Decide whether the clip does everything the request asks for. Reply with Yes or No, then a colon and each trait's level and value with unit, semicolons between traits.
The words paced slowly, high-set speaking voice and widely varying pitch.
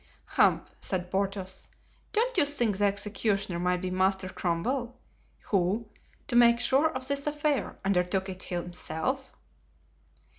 Yes: slow, 125 wpm; high, 200 Hz; wide, 5.8 semitones